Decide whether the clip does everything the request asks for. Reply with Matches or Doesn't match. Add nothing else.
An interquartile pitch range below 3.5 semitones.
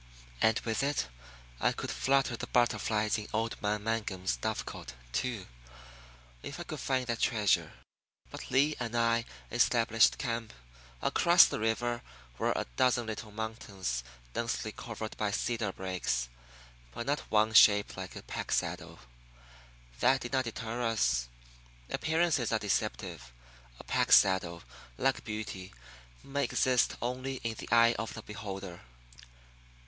Matches